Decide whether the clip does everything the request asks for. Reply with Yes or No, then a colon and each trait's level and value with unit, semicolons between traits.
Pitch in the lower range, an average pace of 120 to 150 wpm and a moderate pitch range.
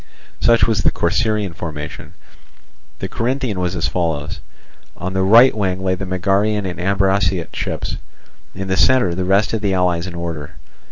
No: very low, 95 Hz; average, 165 wpm; average, 3.0 semitones